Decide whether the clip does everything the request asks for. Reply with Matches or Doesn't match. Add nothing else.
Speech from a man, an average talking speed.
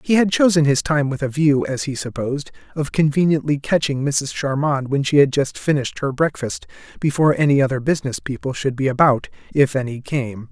Matches